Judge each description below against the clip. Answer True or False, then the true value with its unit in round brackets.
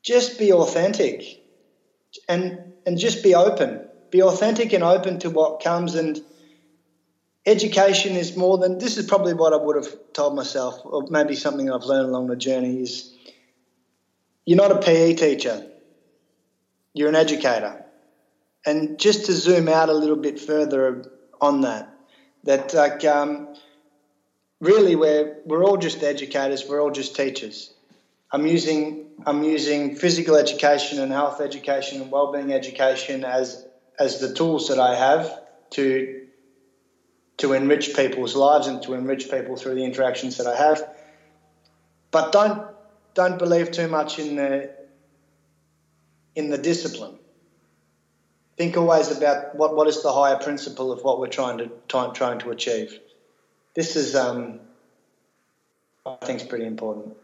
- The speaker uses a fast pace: False (145 wpm)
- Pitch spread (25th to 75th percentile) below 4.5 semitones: True (3.8 semitones)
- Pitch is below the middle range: False (145 Hz)